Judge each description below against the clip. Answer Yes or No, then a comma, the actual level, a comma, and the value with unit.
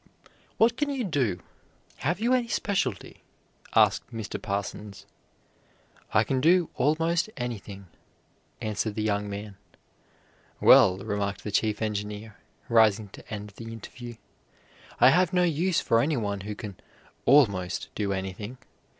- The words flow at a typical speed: No, slow, 130 wpm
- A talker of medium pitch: No, low, 110 Hz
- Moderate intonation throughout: No, wide, 7.0 semitones